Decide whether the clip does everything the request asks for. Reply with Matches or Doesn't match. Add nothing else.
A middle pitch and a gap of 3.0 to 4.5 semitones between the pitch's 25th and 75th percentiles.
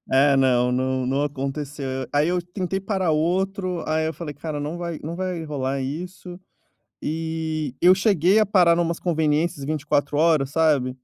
Matches